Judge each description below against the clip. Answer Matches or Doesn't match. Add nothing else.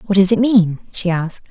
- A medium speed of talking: Doesn't match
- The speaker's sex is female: Matches